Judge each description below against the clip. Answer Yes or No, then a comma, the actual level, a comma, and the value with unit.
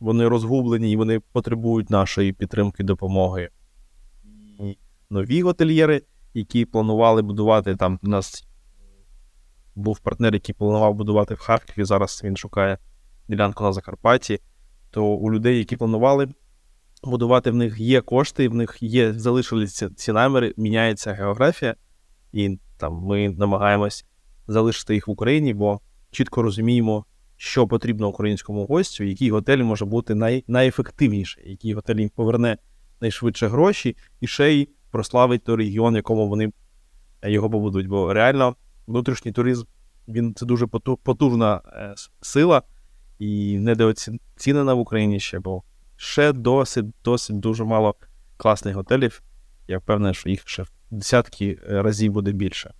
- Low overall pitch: Yes, low, 110 Hz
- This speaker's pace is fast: No, average, 135 wpm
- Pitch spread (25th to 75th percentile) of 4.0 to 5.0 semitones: No, average, 3.0 semitones